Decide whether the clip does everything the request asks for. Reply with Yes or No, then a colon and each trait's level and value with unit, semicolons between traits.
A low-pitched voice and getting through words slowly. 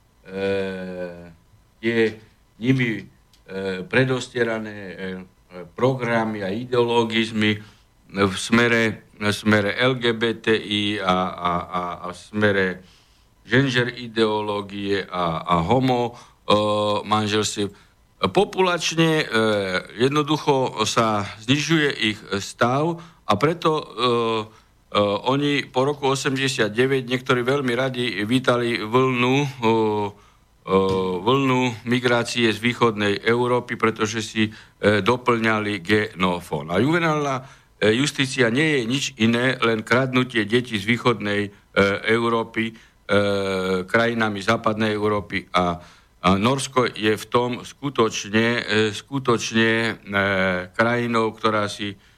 Yes: low, 110 Hz; slow, 100 wpm